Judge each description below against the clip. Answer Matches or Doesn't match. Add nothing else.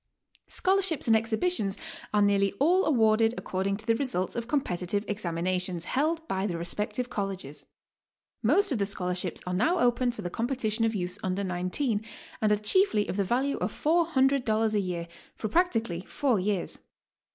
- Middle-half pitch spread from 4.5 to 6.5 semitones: Matches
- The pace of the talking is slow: Doesn't match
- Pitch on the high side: Matches